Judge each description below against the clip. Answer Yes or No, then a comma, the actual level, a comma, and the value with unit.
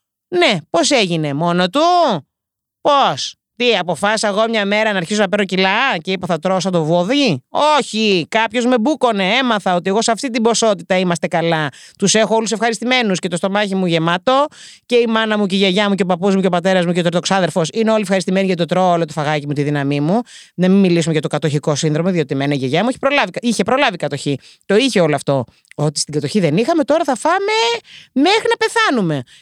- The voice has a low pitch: No, high, 195 Hz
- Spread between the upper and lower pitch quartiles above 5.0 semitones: Yes, wide, 5.4 semitones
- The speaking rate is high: Yes, fast, 220 wpm